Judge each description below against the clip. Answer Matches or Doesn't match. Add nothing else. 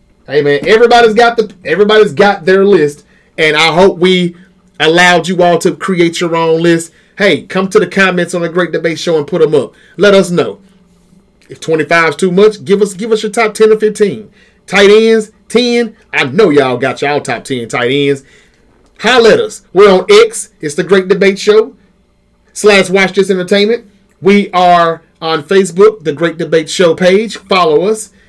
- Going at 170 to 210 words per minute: Matches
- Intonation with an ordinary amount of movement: Matches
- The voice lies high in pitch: Matches